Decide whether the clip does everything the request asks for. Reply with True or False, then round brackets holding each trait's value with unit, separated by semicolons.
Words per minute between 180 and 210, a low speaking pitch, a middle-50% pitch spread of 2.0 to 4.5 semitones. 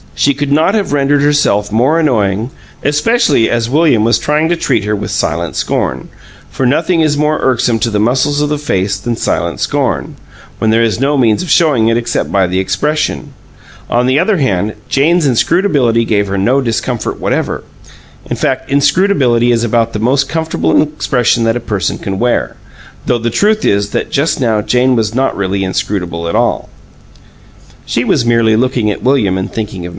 False (190 wpm; 120 Hz; 5.2 semitones)